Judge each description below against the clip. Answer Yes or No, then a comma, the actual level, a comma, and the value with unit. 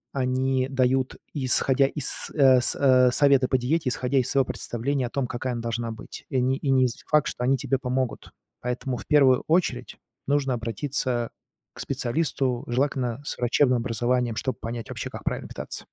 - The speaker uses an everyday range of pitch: No, narrow, 1.8 semitones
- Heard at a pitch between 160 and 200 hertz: No, low, 130 Hz